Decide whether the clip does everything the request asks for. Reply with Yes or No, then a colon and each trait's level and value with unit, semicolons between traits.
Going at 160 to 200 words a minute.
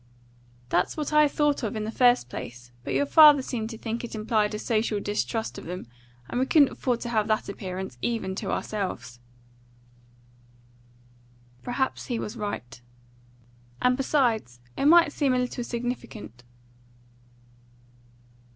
No: average, 145 wpm